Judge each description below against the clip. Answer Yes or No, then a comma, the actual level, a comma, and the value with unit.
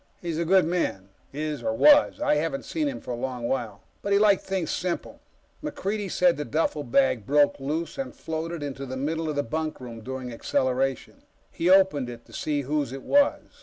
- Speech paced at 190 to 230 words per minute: Yes, average, 195 wpm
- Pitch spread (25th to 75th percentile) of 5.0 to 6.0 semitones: Yes, wide, 5.6 semitones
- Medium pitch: Yes, medium, 150 Hz